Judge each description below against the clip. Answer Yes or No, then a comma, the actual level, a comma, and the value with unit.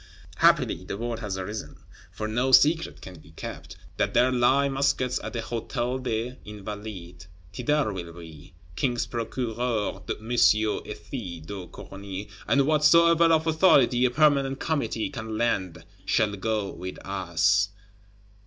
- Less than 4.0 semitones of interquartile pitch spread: No, average, 5.1 semitones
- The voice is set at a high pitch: No, low, 110 Hz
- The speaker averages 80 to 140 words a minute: Yes, slow, 135 wpm